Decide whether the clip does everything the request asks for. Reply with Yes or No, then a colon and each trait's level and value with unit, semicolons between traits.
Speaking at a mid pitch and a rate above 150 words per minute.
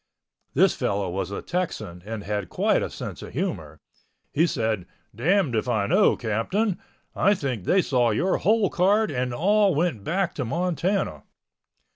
Yes: medium, 145 Hz; average, 160 wpm